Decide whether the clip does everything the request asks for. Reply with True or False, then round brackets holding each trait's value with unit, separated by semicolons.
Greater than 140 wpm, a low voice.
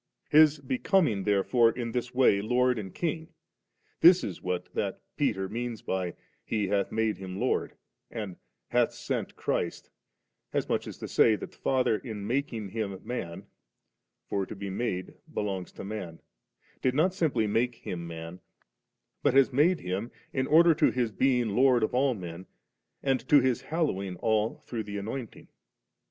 True (165 wpm; 115 Hz)